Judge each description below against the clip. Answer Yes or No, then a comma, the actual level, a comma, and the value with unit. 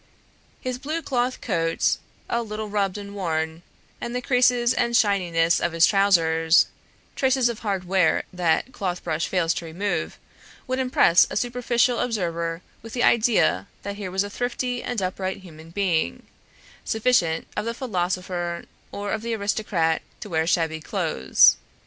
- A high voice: Yes, high, 195 Hz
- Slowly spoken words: No, average, 155 wpm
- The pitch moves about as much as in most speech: No, wide, 5.9 semitones